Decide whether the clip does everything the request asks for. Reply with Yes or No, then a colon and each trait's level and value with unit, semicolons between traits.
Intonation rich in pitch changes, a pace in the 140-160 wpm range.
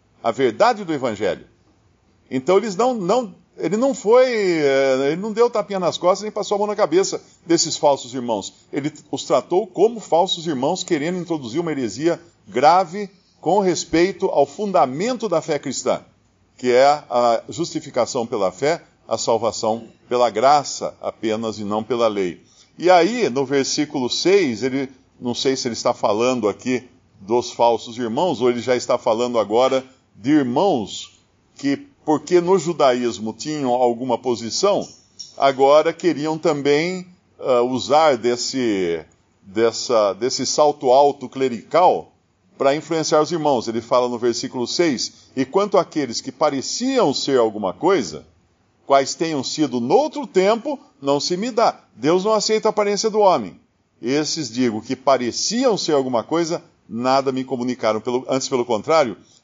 Yes: wide, 6.5 semitones; average, 150 wpm